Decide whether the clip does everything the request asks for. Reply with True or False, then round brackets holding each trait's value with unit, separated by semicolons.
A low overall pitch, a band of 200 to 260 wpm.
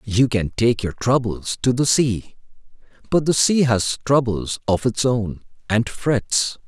False (120 Hz; 160 wpm)